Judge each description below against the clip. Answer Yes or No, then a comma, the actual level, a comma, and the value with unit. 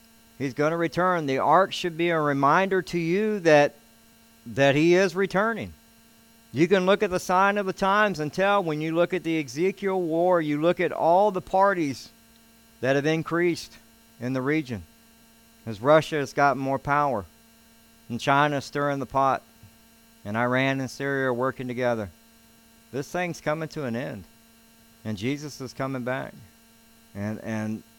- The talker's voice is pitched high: No, low, 135 Hz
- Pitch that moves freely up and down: Yes, wide, 6.7 semitones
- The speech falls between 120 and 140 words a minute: No, average, 170 wpm